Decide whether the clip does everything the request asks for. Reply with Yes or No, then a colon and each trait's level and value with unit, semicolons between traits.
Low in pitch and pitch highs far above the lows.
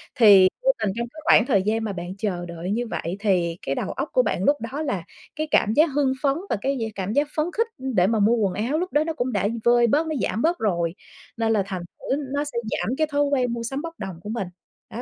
No: high, 235 Hz; wide, 6.4 semitones